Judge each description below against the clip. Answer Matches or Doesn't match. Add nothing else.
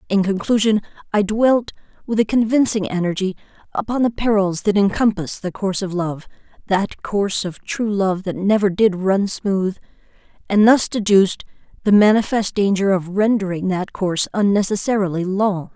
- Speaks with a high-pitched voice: Matches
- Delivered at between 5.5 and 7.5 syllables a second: Doesn't match